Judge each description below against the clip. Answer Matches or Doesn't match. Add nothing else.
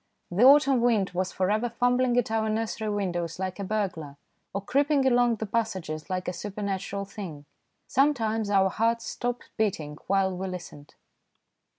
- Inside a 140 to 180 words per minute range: Matches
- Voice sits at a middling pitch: Doesn't match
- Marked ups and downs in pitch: Doesn't match